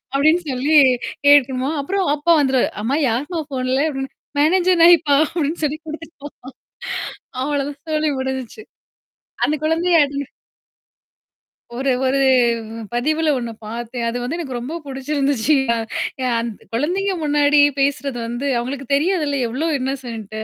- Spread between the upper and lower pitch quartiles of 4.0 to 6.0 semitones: No, average, 3.2 semitones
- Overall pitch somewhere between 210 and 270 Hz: No, very high, 280 Hz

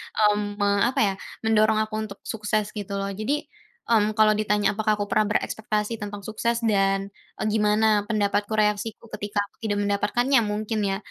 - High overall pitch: Yes, high, 210 Hz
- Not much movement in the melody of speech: Yes, narrow, 1.1 semitones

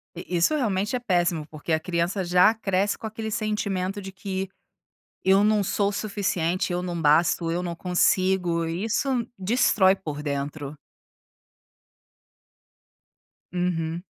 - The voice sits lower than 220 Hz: Yes, medium, 185 Hz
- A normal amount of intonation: Yes, average, 3.3 semitones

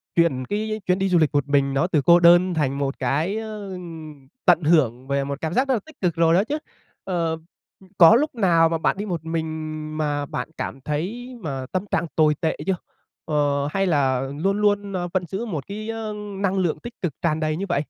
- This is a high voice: No, medium, 170 Hz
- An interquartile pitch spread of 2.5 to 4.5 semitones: No, average, 5.1 semitones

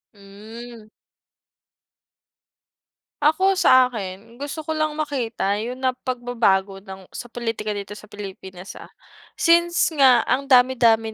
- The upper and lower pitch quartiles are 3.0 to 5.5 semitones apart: Yes, average, 4.3 semitones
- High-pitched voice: Yes, high, 235 Hz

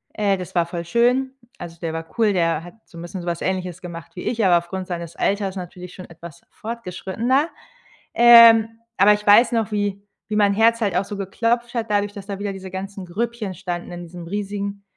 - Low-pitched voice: No, high, 195 Hz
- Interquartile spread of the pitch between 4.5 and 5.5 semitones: No, average, 3.7 semitones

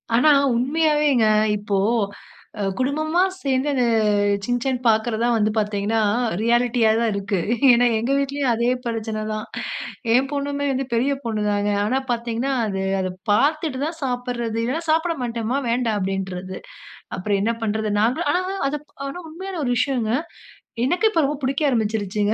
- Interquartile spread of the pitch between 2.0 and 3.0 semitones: No, average, 4.3 semitones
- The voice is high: Yes, high, 240 Hz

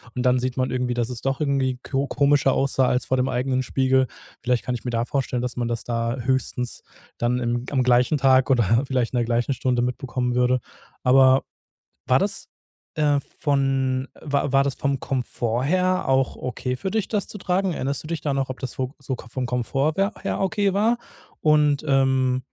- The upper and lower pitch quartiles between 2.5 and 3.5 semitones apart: No, narrow, 2.0 semitones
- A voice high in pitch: No, low, 130 Hz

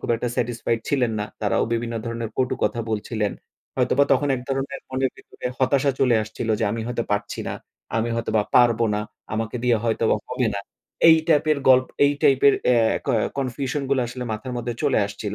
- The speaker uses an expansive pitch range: No, average, 2.8 semitones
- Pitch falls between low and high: No, low, 120 Hz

